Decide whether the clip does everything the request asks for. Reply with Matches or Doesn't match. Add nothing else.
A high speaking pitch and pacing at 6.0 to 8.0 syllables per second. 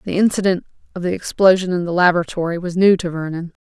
Doesn't match